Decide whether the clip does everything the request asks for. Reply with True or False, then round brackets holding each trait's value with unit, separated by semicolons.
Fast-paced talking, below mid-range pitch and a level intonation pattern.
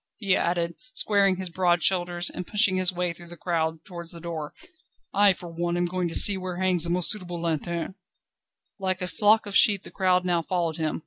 False (215 wpm; 175 Hz; 1.6 semitones)